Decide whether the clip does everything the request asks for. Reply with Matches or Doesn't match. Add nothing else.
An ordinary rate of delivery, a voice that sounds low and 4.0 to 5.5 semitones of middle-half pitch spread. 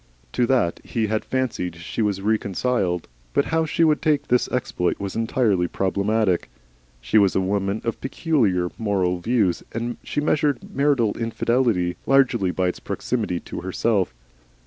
Matches